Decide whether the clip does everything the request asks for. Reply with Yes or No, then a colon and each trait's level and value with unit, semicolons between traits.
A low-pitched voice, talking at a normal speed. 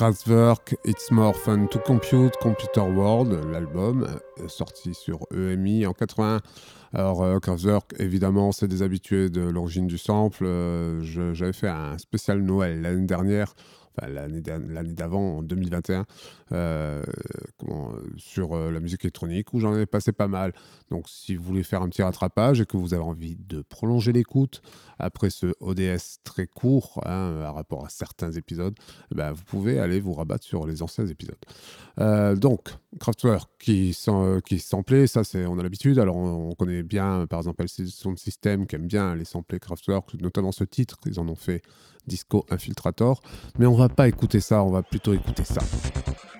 Yes: very low, 95 Hz; average, 175 wpm